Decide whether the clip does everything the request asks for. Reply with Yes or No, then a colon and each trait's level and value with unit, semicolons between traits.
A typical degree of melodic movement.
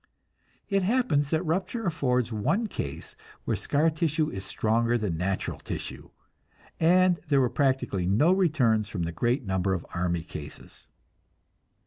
No: wide, 8.9 semitones